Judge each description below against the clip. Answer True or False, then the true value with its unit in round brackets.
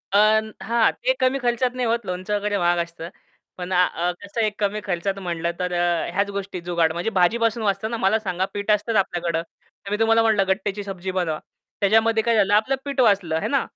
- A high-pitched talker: True (200 Hz)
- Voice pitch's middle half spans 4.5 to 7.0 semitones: False (3.8 semitones)